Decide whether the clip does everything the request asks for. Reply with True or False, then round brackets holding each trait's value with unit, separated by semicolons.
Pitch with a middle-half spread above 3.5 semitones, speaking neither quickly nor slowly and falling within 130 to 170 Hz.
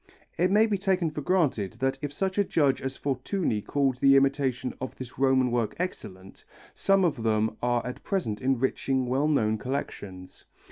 True (4.5 semitones; 175 wpm; 135 Hz)